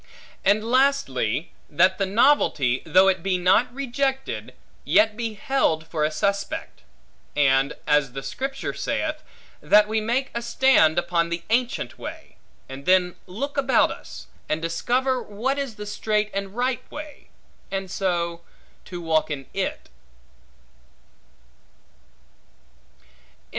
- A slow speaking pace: Yes, slow, 125 wpm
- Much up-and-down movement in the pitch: Yes, wide, 7.2 semitones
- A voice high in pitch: Yes, high, 200 Hz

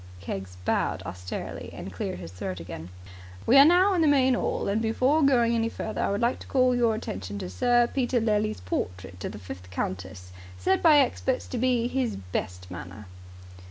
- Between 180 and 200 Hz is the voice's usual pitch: No, high, 215 Hz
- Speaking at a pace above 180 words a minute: Yes, average, 195 wpm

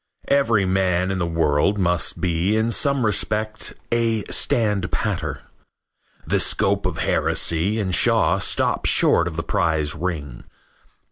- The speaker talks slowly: Yes, slow, 130 wpm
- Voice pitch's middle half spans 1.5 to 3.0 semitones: No, average, 4.5 semitones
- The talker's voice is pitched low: Yes, very low, 95 Hz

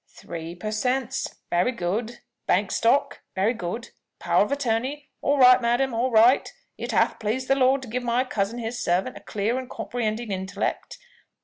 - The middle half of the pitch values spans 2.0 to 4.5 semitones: Yes, average, 3.5 semitones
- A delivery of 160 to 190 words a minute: Yes, average, 175 wpm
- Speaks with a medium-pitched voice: No, high, 235 Hz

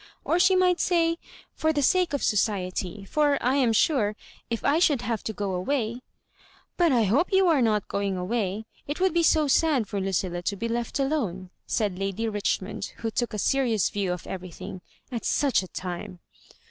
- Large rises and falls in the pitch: Yes, wide, 6.8 semitones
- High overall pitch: Yes, high, 230 Hz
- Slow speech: No, average, 195 wpm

